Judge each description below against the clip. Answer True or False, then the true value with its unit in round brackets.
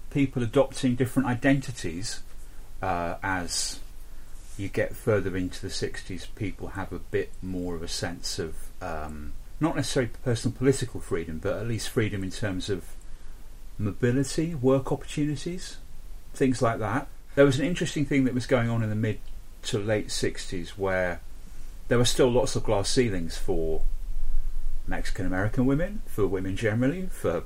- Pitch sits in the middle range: False (105 Hz)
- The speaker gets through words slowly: False (155 wpm)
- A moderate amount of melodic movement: False (6.7 semitones)